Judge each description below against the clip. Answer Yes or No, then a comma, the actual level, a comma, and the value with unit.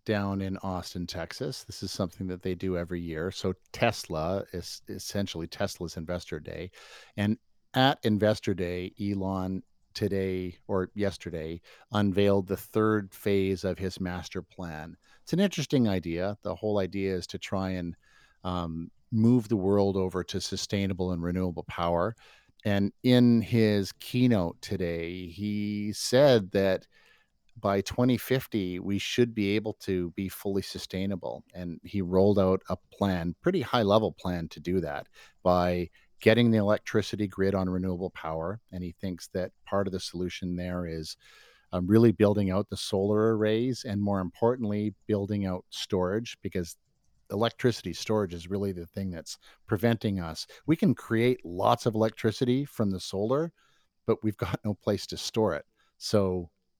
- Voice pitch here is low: Yes, low, 100 Hz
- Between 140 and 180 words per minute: Yes, average, 155 wpm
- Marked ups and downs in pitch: No, average, 3.0 semitones